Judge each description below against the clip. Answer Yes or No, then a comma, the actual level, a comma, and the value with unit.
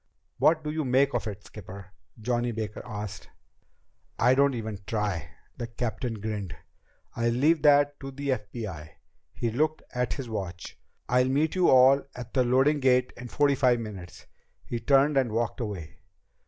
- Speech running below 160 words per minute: No, average, 165 wpm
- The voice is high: No, low, 120 Hz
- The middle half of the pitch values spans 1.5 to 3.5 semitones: No, average, 4.2 semitones